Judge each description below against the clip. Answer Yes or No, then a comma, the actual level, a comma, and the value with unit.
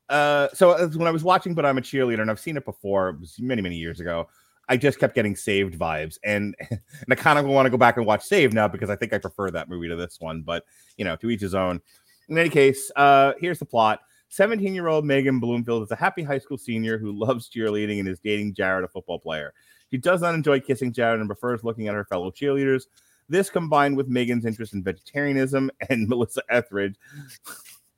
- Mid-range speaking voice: No, low, 115 Hz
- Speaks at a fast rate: Yes, fast, 230 wpm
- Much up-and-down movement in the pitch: Yes, wide, 5.8 semitones